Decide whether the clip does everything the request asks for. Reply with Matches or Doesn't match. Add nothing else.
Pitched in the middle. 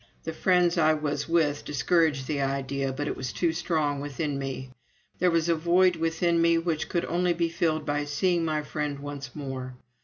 Matches